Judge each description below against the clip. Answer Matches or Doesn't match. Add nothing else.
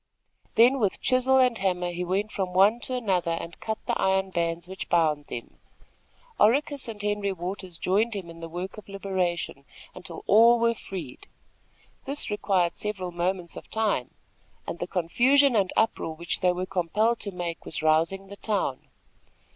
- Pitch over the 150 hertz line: Matches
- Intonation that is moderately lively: Matches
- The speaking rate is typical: Matches